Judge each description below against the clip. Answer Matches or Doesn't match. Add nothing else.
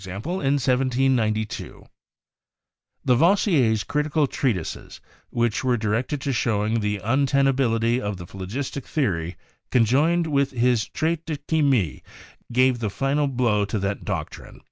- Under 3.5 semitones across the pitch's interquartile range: Doesn't match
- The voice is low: Matches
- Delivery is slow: Matches